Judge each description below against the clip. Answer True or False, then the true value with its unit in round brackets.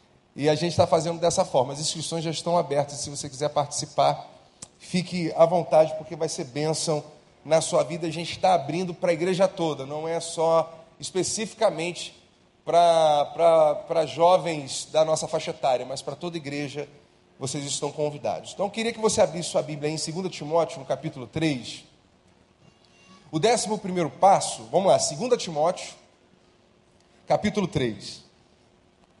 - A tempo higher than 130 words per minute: True (155 wpm)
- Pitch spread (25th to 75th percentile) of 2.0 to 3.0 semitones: True (2.7 semitones)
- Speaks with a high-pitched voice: False (160 Hz)